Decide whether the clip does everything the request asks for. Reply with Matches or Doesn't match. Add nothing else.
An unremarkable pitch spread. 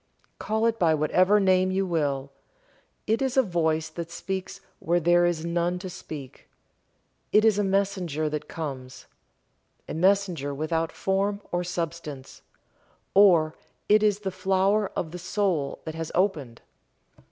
Matches